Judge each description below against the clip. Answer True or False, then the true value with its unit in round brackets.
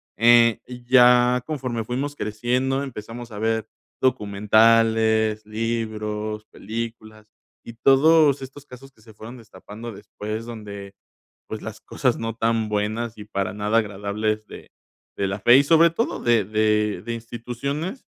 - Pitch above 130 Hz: False (115 Hz)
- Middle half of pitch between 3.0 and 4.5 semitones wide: False (2.4 semitones)